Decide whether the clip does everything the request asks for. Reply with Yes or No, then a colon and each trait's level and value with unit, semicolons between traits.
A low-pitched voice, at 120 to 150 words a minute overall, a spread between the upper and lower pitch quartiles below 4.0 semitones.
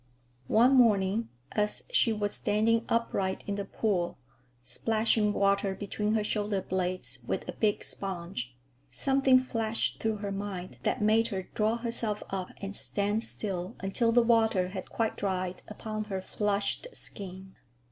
No: high, 210 Hz; average, 145 wpm; average, 2.7 semitones